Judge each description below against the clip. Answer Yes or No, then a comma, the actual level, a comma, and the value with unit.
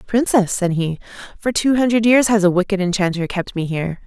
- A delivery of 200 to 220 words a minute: Yes, fast, 205 wpm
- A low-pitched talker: No, high, 200 Hz